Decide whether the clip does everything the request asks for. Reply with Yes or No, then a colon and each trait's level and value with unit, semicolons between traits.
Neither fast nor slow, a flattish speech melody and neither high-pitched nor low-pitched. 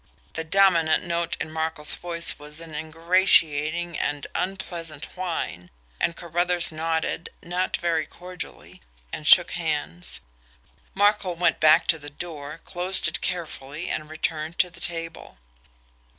No: slow, 130 wpm; narrow, 2.1 semitones; medium, 165 Hz